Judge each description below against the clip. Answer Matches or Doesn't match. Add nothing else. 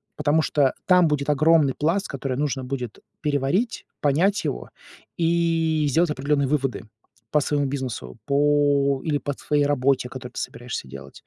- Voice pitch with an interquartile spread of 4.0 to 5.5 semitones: Doesn't match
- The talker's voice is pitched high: Doesn't match